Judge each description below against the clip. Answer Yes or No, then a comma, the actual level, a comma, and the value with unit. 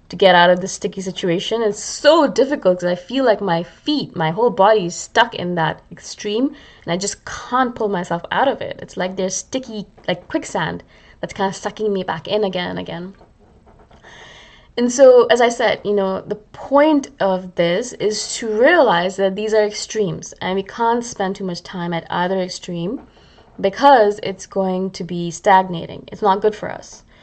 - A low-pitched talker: No, high, 195 Hz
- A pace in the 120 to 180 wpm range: No, average, 195 wpm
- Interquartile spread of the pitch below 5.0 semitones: Yes, average, 3.4 semitones